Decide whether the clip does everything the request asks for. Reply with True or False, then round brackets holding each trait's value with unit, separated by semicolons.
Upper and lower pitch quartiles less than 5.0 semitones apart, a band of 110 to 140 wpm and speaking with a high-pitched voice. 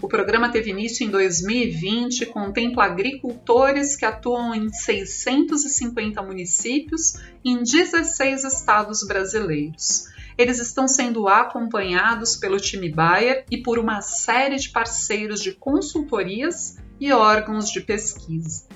True (4.2 semitones; 120 wpm; 235 Hz)